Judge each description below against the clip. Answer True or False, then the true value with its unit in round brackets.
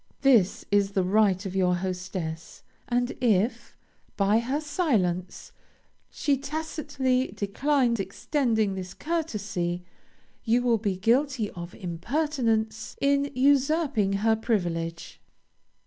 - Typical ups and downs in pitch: False (6.4 semitones)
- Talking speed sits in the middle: False (105 wpm)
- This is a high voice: True (220 Hz)